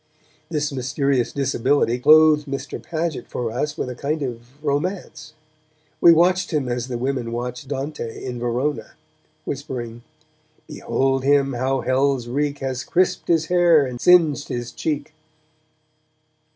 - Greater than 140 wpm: No, slow, 135 wpm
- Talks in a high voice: No, medium, 140 Hz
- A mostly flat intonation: No, average, 3.4 semitones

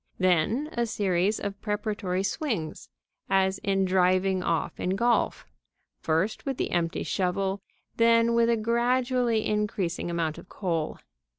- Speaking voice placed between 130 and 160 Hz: No, high, 195 Hz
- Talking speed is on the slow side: Yes, slow, 130 wpm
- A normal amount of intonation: Yes, average, 4.1 semitones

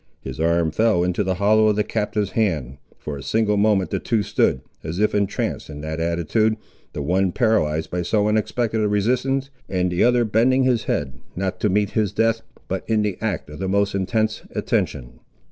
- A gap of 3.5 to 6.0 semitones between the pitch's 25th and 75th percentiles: Yes, average, 4.3 semitones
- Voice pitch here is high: No, low, 100 Hz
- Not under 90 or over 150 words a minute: No, average, 195 wpm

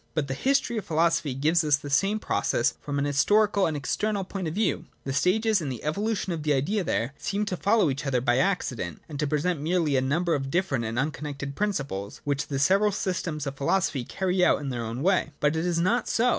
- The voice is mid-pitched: Yes, medium, 155 Hz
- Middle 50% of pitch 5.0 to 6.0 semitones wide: Yes, wide, 5.6 semitones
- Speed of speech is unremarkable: No, fast, 235 wpm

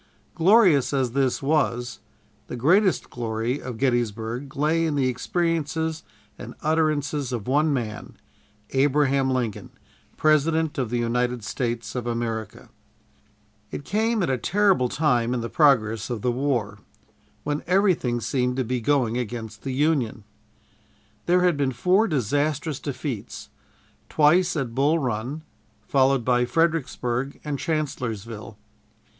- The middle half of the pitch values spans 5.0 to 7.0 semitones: No, average, 4.3 semitones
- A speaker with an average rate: No, slow, 130 wpm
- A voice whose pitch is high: No, low, 135 Hz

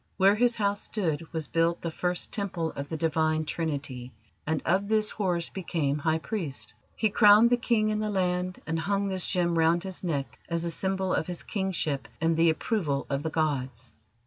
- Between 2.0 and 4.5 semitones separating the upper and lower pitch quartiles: Yes, average, 3.9 semitones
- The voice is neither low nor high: Yes, medium, 170 Hz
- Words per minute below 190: No, average, 195 wpm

